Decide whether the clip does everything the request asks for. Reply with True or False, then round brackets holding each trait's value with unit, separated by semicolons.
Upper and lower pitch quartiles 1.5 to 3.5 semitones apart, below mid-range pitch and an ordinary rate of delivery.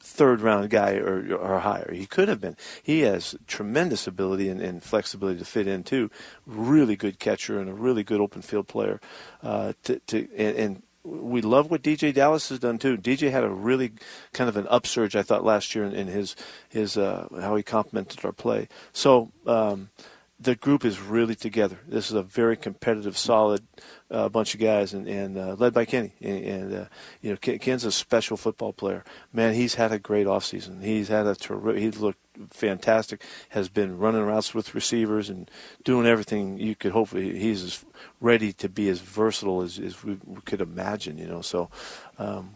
True (2.5 semitones; 110 Hz; 195 wpm)